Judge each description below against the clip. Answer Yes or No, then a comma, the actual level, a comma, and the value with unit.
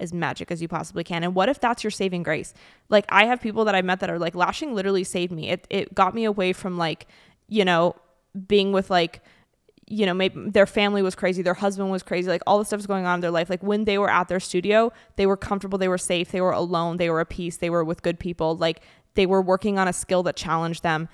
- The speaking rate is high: Yes, fast, 265 wpm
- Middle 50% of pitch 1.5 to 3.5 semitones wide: Yes, narrow, 2.5 semitones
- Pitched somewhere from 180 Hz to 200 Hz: Yes, medium, 185 Hz